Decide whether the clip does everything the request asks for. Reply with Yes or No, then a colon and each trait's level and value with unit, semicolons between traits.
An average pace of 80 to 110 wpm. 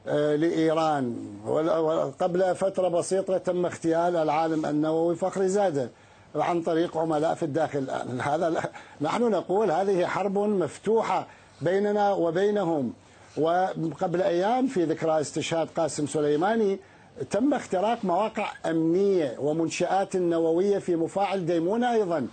Yes: average, 105 wpm